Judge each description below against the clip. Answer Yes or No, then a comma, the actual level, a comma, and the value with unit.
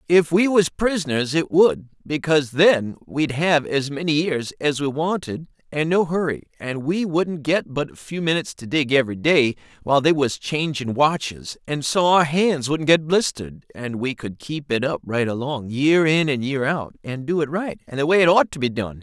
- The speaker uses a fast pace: Yes, fast, 215 wpm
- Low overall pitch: No, medium, 145 Hz